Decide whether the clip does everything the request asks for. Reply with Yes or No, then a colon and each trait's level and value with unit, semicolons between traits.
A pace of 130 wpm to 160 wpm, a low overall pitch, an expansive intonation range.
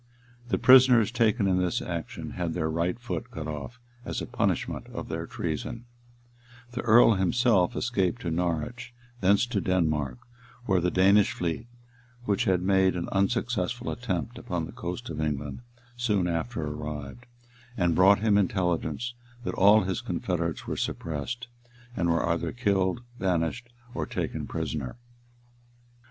Yes: average, 145 wpm; very low, 95 Hz; wide, 5.7 semitones